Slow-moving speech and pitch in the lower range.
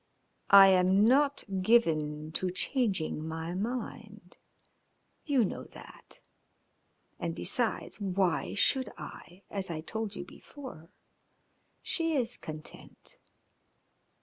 No: slow, 100 wpm; high, 195 Hz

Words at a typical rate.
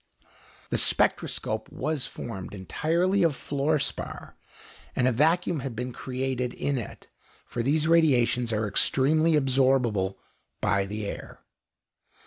No: slow, 120 wpm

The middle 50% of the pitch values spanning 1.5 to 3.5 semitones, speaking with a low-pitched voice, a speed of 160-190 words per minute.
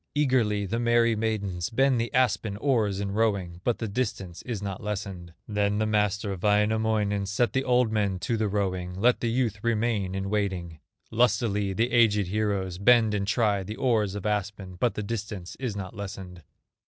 Yes: average, 2.7 semitones; low, 105 Hz; average, 180 wpm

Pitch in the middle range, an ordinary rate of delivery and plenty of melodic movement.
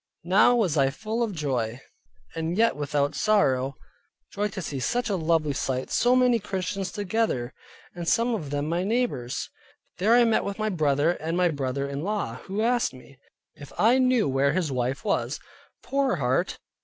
Yes: medium, 170 Hz; average, 180 wpm; wide, 7.6 semitones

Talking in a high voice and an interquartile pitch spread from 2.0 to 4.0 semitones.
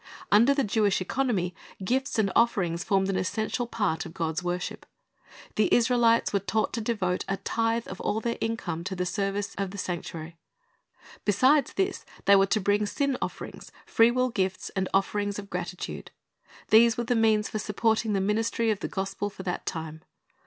Yes: high, 205 Hz; average, 3.4 semitones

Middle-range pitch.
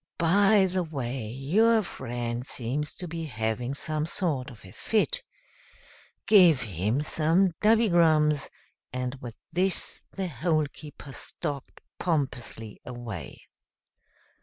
Yes: medium, 150 Hz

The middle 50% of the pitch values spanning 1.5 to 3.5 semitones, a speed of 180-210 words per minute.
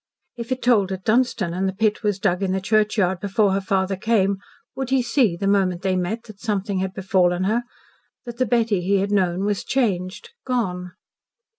Yes: average, 3.1 semitones; average, 195 wpm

